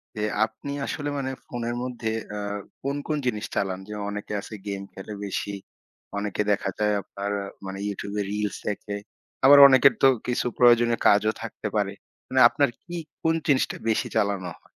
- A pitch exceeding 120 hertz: No, low, 105 Hz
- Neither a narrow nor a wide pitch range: Yes, average, 3.7 semitones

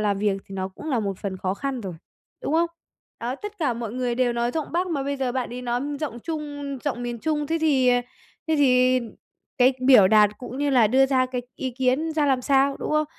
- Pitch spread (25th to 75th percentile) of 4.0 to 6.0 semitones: No, average, 3.3 semitones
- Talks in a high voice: Yes, very high, 255 Hz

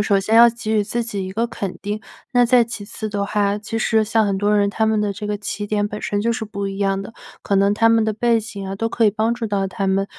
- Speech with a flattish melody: Yes, narrow, 2.0 semitones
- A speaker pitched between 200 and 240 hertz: Yes, high, 210 Hz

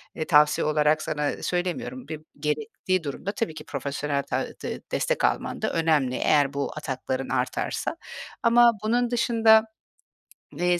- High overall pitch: No, medium, 155 Hz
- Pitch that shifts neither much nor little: No, wide, 6.9 semitones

